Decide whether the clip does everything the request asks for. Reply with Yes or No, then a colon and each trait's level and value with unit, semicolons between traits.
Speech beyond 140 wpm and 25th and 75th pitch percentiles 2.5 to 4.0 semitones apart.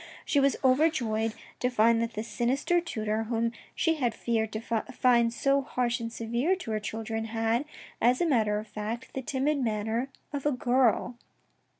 Yes: average, 180 wpm; average, 2.9 semitones